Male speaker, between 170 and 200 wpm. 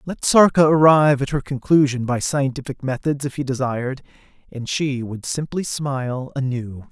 No: male; average, 155 wpm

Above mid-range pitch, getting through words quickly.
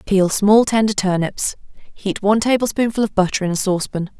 No: high, 205 Hz; average, 170 wpm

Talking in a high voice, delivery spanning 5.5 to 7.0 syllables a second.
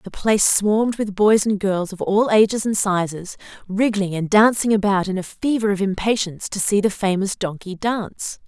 No: high, 200 Hz; 5.1 syllables/s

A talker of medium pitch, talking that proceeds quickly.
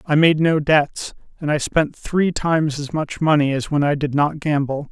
Yes: medium, 150 Hz; fast, 220 wpm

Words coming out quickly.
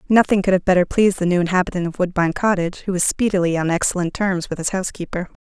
Yes: fast, 220 wpm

